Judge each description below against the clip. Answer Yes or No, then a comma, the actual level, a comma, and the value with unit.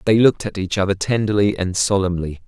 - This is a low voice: Yes, very low, 95 Hz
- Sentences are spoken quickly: No, average, 195 wpm